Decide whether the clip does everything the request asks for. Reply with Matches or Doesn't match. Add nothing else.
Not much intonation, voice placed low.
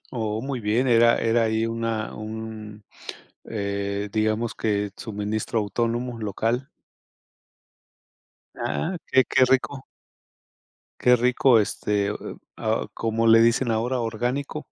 Matches